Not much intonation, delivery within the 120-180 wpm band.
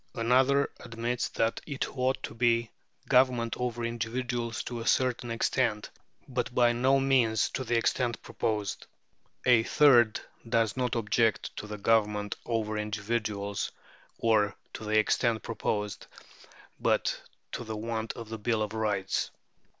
Yes: narrow, 2.2 semitones; average, 140 wpm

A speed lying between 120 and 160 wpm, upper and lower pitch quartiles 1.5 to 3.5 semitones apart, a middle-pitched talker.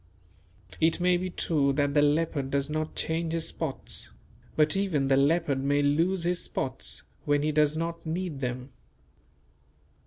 Yes: average, 155 wpm; average, 2.9 semitones; medium, 155 Hz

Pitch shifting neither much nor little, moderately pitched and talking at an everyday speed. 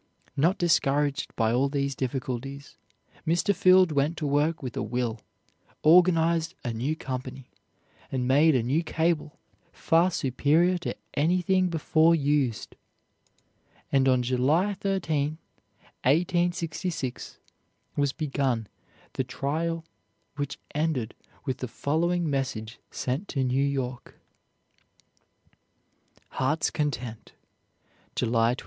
No: average, 4.3 semitones; medium, 145 Hz; slow, 110 wpm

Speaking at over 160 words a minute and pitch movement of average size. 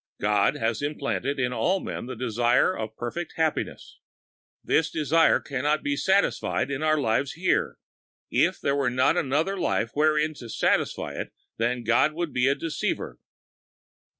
No: average, 155 wpm; average, 4.1 semitones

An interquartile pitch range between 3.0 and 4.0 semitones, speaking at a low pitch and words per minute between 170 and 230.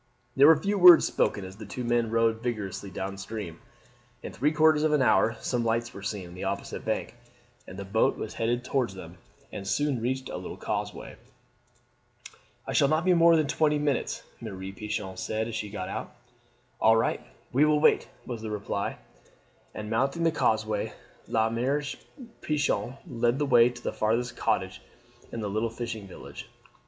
No: average, 4.7 semitones; low, 115 Hz; average, 185 wpm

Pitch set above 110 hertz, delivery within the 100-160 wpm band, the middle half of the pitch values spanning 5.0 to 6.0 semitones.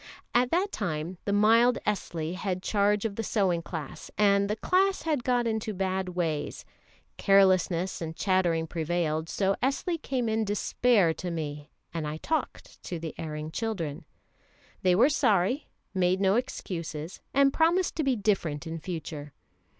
Yes: high, 190 Hz; average, 155 wpm; wide, 5.4 semitones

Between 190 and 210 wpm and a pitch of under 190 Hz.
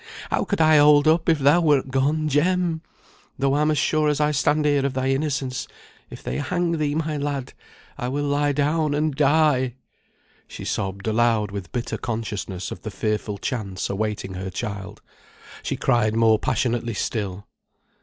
No: average, 170 wpm; low, 135 Hz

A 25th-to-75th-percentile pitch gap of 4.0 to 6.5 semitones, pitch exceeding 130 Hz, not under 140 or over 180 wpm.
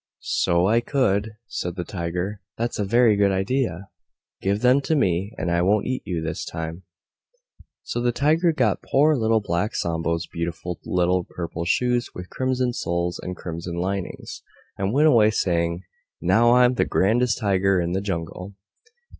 No: wide, 5.5 semitones; very low, 95 Hz; average, 165 wpm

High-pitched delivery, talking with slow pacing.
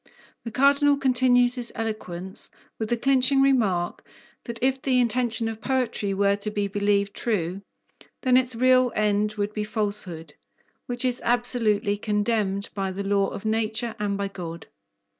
No: high, 220 Hz; average, 155 wpm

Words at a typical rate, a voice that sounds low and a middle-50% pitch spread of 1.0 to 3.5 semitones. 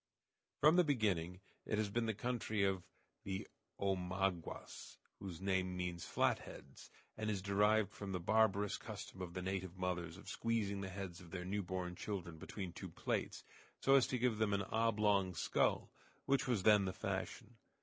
Yes: average, 170 wpm; low, 100 Hz; average, 2.8 semitones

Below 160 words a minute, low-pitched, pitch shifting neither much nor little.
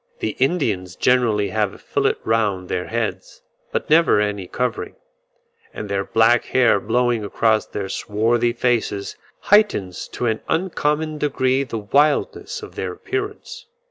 No: average, 140 wpm; low, 120 Hz; wide, 5.9 semitones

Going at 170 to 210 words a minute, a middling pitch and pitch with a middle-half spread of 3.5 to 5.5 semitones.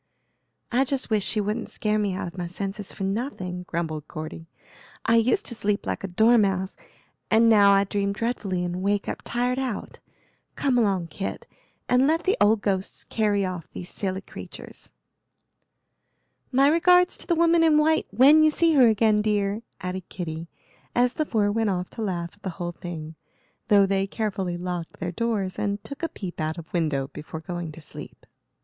No: average, 185 wpm; high, 200 Hz; average, 4.5 semitones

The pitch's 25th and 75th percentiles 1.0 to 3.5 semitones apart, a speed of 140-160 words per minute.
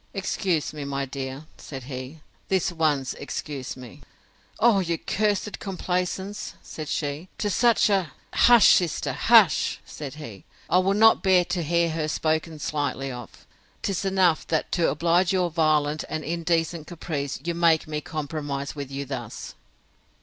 No: average, 4.0 semitones; average, 150 wpm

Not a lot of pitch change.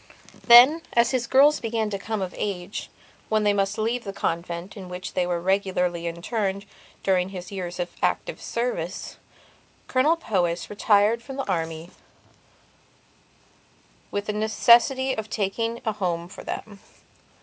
No: average, 4.4 semitones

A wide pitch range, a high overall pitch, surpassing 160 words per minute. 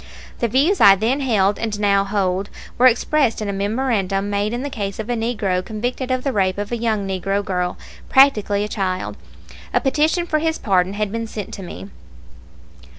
No: average, 3.9 semitones; high, 210 Hz; average, 190 wpm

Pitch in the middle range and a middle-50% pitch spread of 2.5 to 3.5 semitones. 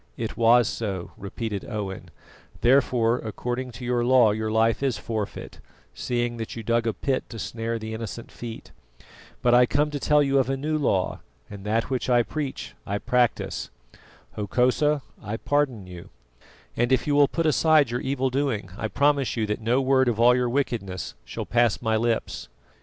No: low, 120 Hz; average, 3.1 semitones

